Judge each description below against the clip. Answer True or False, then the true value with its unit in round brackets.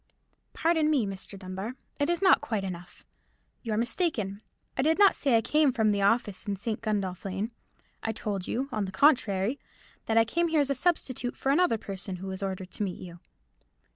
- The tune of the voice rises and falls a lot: True (6.2 semitones)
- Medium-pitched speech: False (220 Hz)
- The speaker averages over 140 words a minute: True (200 wpm)